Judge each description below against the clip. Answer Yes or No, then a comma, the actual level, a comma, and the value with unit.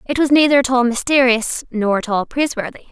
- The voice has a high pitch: Yes, very high, 250 Hz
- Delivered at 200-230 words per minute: Yes, fast, 205 wpm